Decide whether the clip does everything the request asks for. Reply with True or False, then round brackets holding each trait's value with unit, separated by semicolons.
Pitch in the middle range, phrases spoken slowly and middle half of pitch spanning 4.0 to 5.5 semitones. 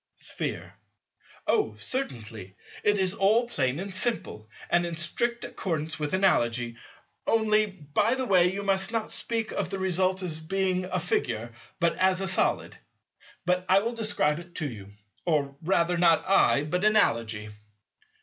False (180 Hz; 150 wpm; 4.7 semitones)